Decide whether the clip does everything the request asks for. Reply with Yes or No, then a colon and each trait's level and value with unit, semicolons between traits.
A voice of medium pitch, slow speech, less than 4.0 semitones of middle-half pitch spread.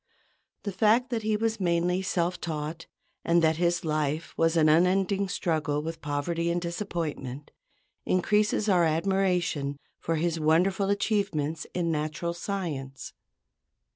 Yes: medium, 170 Hz; slow, 130 wpm; average, 3.6 semitones